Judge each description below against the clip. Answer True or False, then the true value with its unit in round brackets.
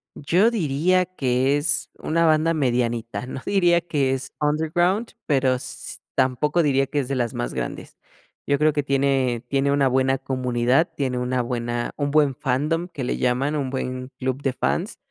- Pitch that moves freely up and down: False (3.2 semitones)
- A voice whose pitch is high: False (135 Hz)